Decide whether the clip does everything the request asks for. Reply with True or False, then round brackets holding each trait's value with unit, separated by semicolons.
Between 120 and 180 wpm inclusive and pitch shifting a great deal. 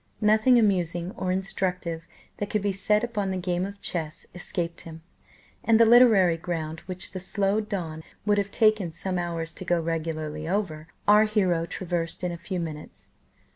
False (175 wpm; 3.6 semitones)